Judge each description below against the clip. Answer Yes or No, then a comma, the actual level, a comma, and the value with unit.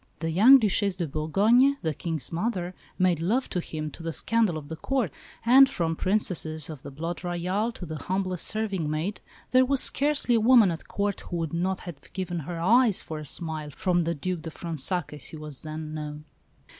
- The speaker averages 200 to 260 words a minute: Yes, fast, 205 wpm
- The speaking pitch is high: No, medium, 175 Hz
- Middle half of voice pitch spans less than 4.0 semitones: No, average, 4.6 semitones